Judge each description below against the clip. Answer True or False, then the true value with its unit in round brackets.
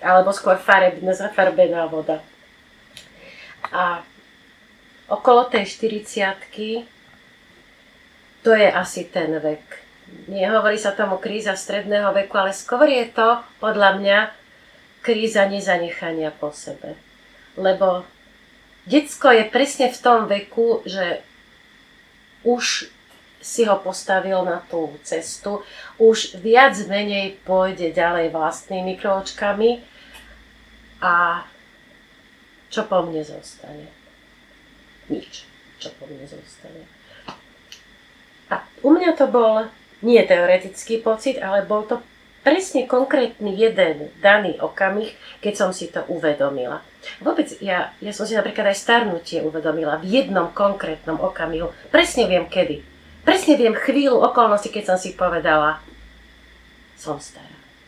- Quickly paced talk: False (110 wpm)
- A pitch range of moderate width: True (4.4 semitones)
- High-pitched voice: True (200 Hz)